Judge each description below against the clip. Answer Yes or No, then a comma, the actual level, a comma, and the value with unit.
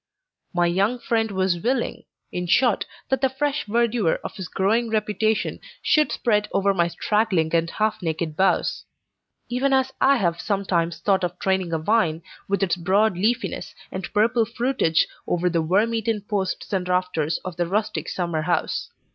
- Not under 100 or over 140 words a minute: No, average, 165 wpm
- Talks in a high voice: Yes, high, 195 Hz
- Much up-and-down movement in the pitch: No, average, 4.5 semitones